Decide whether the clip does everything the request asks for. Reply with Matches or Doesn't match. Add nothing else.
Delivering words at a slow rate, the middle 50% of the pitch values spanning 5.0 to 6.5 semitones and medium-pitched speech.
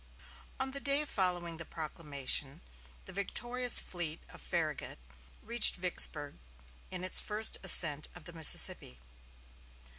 Matches